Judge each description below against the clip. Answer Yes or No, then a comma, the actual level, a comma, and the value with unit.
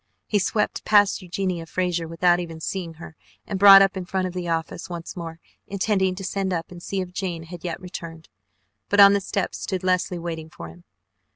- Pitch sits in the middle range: Yes, medium, 180 Hz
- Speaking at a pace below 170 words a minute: No, fast, 205 wpm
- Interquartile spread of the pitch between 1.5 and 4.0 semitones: Yes, narrow, 2.4 semitones